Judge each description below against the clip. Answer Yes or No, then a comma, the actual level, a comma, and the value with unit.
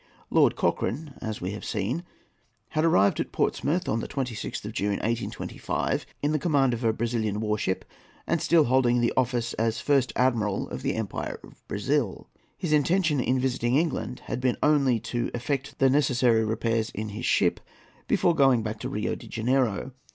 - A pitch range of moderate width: Yes, average, 3.7 semitones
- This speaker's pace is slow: No, average, 175 wpm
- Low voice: Yes, low, 120 Hz